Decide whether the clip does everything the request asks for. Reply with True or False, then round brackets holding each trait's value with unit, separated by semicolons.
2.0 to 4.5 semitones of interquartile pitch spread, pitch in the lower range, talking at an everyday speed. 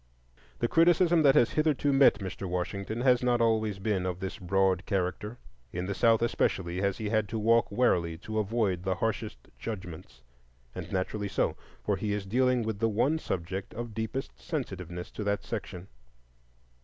True (3.9 semitones; 105 Hz; 165 wpm)